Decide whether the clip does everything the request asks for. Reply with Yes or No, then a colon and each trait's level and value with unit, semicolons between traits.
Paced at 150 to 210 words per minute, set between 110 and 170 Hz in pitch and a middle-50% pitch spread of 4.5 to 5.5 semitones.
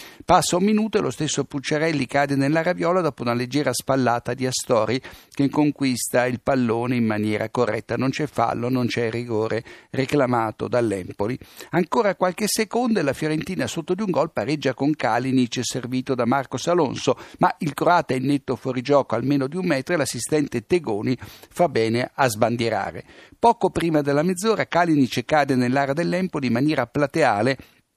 Yes: average, 165 wpm; medium, 140 Hz; average, 5.1 semitones